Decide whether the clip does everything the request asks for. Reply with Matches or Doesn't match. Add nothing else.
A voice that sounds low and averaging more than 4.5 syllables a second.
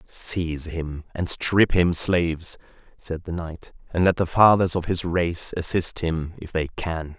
Doesn't match